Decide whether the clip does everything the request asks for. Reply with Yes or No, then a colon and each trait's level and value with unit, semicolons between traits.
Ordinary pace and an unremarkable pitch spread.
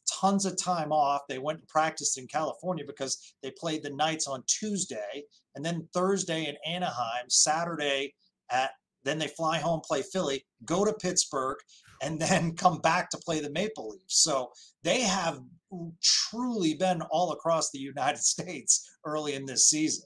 Yes: average, 170 wpm; average, 3.9 semitones